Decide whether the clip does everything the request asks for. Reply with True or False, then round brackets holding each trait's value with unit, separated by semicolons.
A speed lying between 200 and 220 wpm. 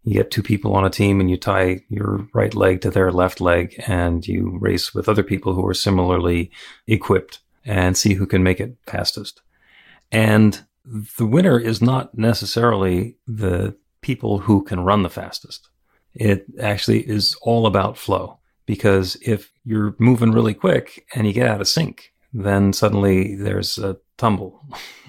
False (165 wpm)